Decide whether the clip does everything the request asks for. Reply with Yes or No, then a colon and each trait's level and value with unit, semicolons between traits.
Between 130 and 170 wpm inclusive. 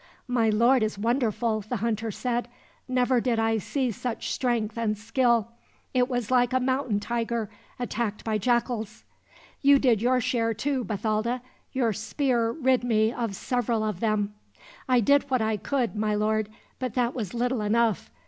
Yes: average, 165 wpm